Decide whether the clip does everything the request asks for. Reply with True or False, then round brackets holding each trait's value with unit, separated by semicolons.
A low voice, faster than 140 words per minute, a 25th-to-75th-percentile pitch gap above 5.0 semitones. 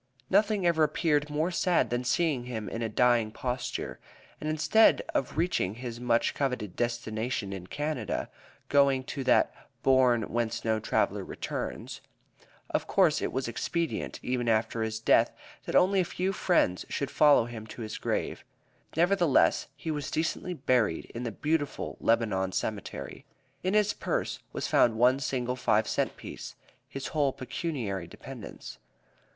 True (125 Hz; 150 wpm; 5.4 semitones)